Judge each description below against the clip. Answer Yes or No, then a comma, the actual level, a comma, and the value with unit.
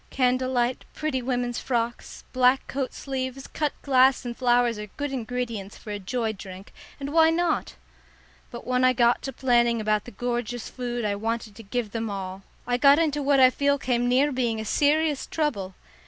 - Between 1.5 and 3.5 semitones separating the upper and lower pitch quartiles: Yes, average, 2.7 semitones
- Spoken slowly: No, average, 185 wpm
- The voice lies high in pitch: Yes, high, 245 Hz